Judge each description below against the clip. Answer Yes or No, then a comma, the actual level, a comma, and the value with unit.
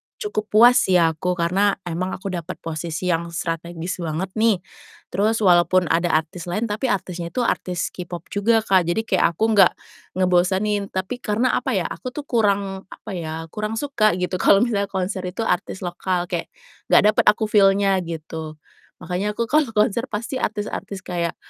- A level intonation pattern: No, average, 3.4 semitones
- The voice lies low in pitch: No, high, 190 Hz